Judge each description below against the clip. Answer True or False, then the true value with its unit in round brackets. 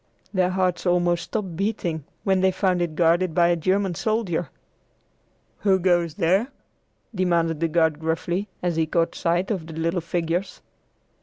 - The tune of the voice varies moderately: False (2.1 semitones)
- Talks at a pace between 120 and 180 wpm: True (155 wpm)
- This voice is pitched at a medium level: True (175 Hz)